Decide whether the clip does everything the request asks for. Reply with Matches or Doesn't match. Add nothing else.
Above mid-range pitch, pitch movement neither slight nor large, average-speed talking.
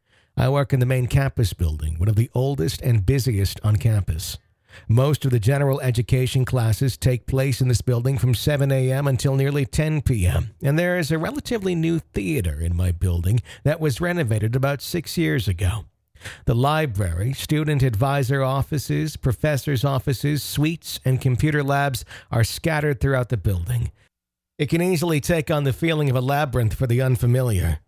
Doesn't match